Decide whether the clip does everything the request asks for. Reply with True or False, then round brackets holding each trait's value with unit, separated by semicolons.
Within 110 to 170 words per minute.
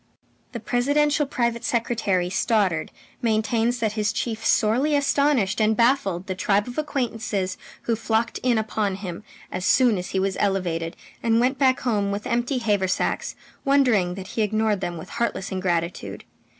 True (155 wpm)